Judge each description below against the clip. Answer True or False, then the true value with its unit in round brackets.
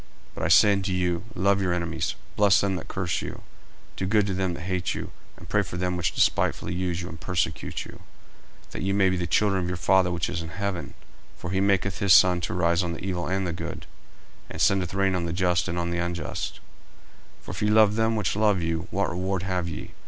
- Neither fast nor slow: False (250 wpm)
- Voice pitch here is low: True (90 Hz)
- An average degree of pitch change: False (2.0 semitones)